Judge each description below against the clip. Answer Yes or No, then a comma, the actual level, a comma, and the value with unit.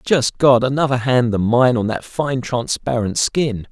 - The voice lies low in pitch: Yes, low, 125 Hz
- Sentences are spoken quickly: No, average, 180 wpm